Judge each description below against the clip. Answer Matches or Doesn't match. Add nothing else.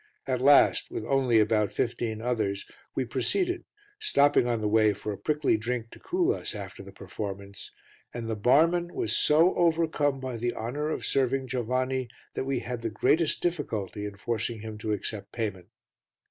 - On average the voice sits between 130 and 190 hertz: Doesn't match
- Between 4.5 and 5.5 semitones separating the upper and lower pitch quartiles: Matches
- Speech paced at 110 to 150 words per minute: Doesn't match